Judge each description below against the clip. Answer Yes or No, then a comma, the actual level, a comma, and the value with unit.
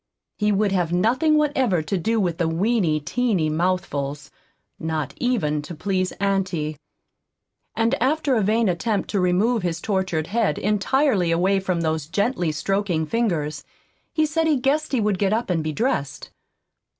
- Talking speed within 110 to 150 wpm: No, average, 160 wpm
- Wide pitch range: Yes, wide, 5.9 semitones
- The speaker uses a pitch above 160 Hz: Yes, high, 190 Hz